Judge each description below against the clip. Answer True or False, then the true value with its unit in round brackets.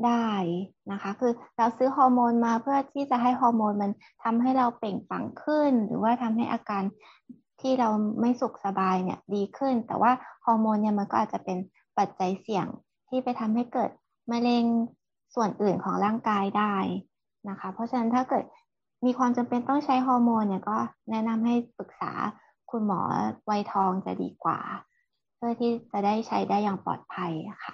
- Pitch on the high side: True (230 Hz)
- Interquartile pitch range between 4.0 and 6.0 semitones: False (3.3 semitones)